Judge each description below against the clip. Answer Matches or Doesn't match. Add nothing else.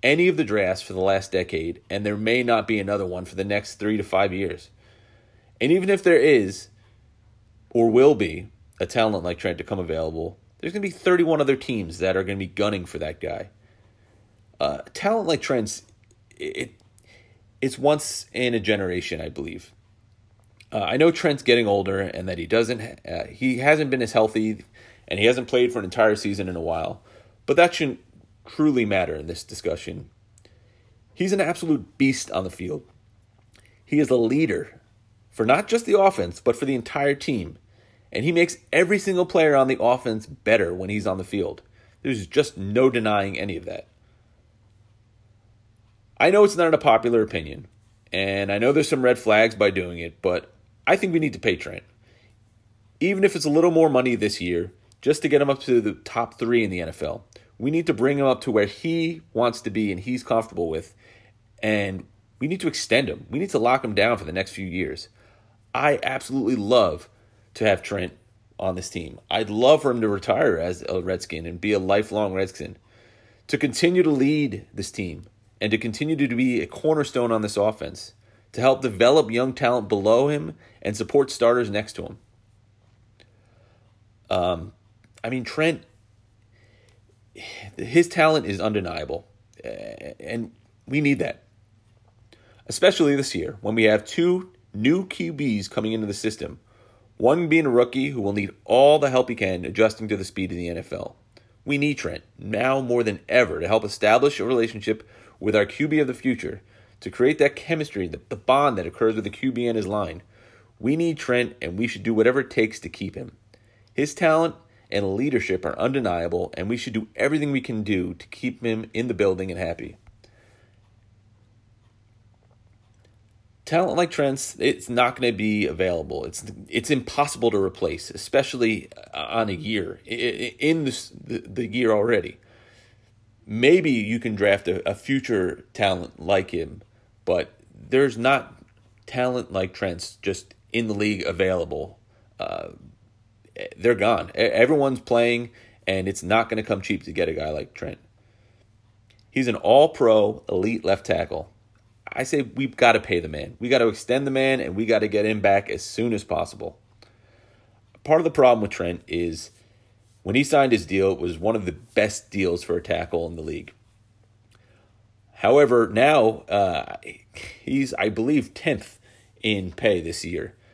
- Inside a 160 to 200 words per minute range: Matches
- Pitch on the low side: Matches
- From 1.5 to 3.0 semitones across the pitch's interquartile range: Doesn't match